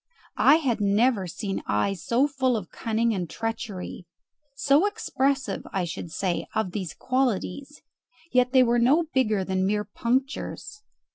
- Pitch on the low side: No, high, 230 Hz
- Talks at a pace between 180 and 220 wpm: No, average, 145 wpm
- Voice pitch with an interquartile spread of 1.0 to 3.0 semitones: No, average, 5.3 semitones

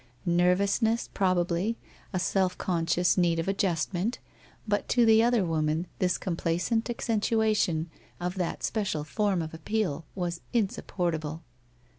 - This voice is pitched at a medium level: Yes, medium, 180 Hz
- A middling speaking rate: No, slow, 125 wpm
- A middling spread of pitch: Yes, average, 3.9 semitones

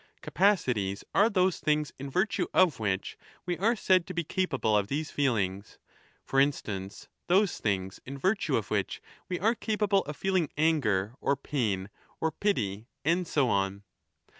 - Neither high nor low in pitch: Yes, medium, 145 Hz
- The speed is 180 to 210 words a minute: No, average, 165 wpm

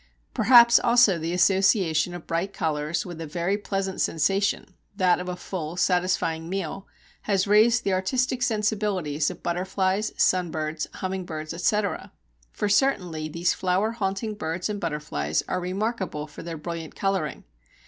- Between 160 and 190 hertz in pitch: Yes, medium, 185 Hz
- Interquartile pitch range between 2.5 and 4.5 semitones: Yes, average, 3.5 semitones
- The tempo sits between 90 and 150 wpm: Yes, average, 145 wpm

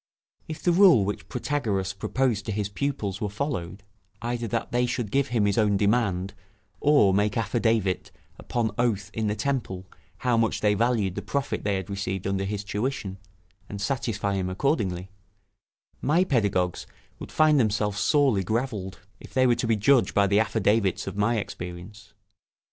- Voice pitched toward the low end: Yes, low, 105 Hz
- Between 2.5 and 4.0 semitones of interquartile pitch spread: Yes, average, 3.7 semitones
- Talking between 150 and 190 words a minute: Yes, average, 165 wpm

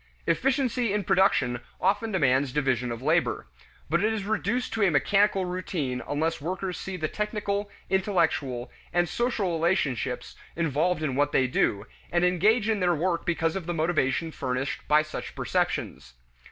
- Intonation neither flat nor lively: No, wide, 5.8 semitones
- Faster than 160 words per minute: No, average, 155 wpm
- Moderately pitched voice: Yes, medium, 175 Hz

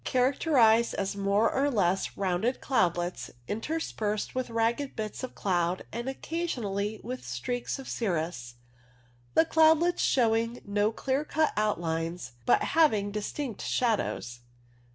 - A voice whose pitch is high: Yes, high, 220 Hz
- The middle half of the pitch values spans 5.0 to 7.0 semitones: Yes, average, 5.3 semitones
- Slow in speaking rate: Yes, slow, 125 wpm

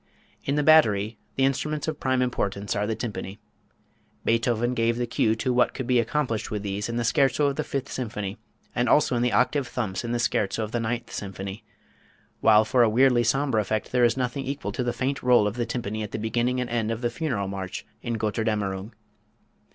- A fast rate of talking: Yes, fast, 215 wpm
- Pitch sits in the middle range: No, low, 120 Hz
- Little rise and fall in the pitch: No, average, 3.0 semitones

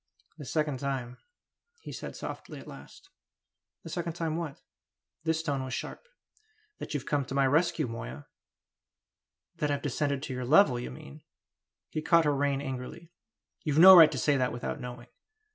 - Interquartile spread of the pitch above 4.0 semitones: No, average, 3.6 semitones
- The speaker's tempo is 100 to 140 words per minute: No, average, 170 wpm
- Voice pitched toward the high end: No, medium, 145 Hz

